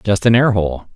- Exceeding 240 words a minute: Yes, fast, 250 wpm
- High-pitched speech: No, low, 105 Hz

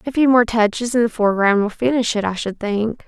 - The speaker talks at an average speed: No, fast, 255 wpm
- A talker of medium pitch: No, high, 225 Hz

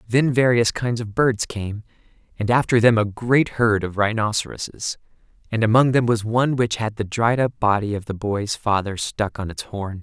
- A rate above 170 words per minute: Yes, average, 195 wpm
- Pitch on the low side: Yes, low, 110 Hz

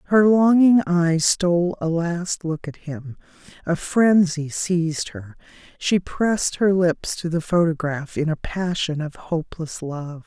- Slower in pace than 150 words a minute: Yes, average, 140 wpm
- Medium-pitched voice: Yes, medium, 170 Hz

